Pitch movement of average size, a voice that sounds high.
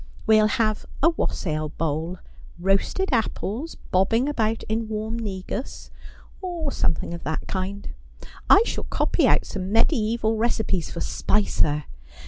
Yes: average, 3.7 semitones; high, 215 Hz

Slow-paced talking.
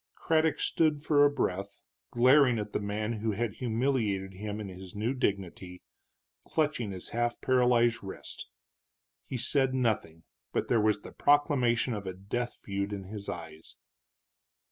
No: average, 150 wpm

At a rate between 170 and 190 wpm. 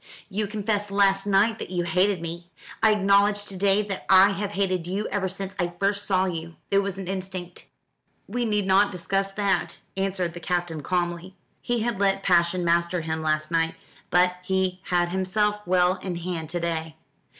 Yes: average, 185 wpm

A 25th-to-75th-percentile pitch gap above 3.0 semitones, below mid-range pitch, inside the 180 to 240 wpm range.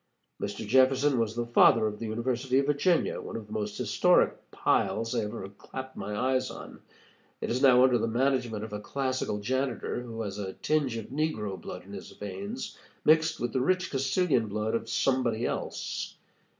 Yes: average, 3.6 semitones; low, 120 Hz; average, 185 wpm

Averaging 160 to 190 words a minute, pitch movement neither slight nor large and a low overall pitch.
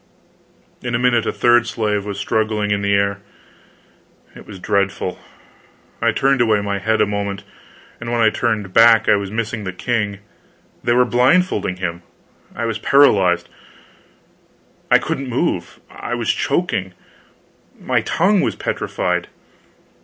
No: average, 140 wpm; average, 3.2 semitones; low, 110 Hz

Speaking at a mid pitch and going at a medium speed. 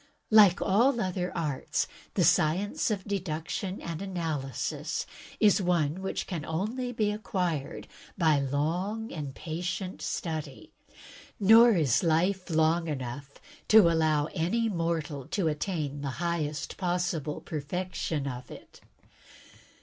No: medium, 170 Hz; slow, 120 wpm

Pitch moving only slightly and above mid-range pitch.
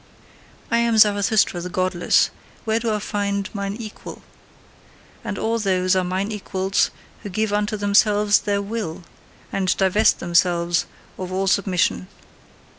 Yes: narrow, 2.3 semitones; high, 200 Hz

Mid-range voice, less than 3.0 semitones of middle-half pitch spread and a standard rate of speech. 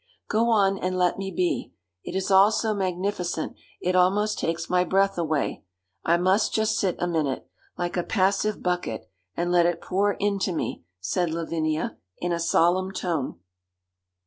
Yes: medium, 180 Hz; narrow, 2.4 semitones; average, 165 wpm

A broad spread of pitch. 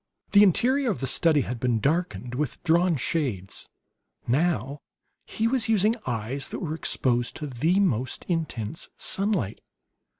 Yes: wide, 6.8 semitones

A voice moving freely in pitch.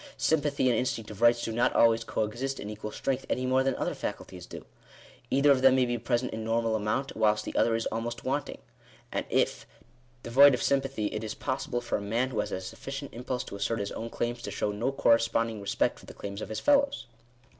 No: average, 3.1 semitones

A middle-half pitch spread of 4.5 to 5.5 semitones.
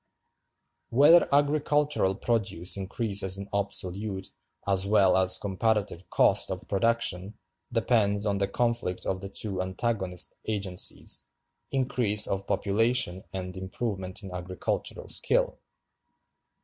No: average, 3.4 semitones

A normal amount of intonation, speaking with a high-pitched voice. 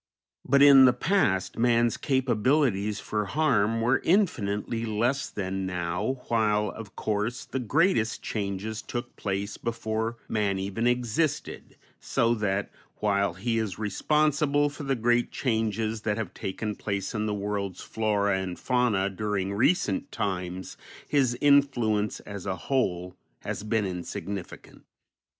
No: average, 3.6 semitones; low, 110 Hz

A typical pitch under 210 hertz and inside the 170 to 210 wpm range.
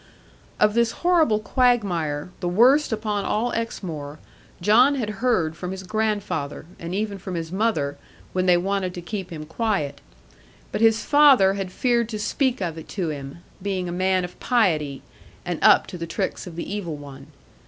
Yes: high, 190 Hz; average, 175 wpm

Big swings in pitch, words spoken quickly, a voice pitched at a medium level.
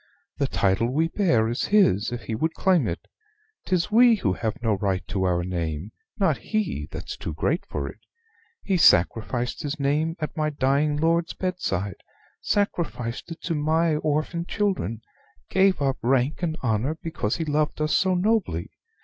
No: wide, 7.4 semitones; average, 165 wpm; medium, 150 Hz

